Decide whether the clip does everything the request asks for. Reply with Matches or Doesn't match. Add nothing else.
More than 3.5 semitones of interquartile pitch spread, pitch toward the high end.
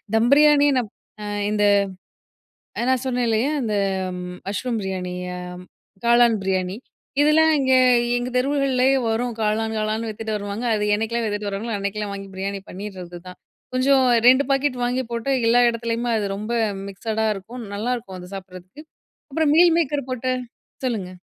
Matches